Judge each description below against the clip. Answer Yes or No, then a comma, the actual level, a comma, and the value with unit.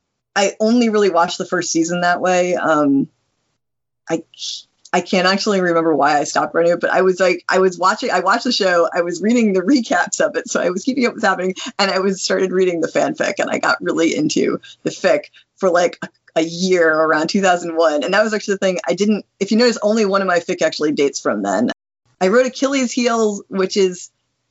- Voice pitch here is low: No, medium, 185 Hz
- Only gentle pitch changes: No, average, 3.7 semitones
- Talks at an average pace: No, fast, 225 wpm